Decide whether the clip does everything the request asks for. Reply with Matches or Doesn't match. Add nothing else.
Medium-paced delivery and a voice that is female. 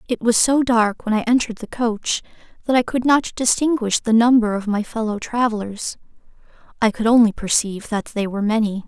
Matches